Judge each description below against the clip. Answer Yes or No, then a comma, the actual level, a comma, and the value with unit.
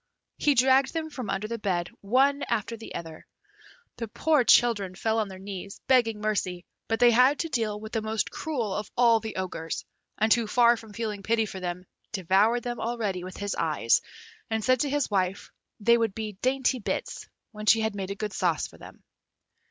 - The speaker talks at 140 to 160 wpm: No, average, 200 wpm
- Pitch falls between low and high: No, high, 220 Hz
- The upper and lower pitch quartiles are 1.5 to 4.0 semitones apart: Yes, average, 3.4 semitones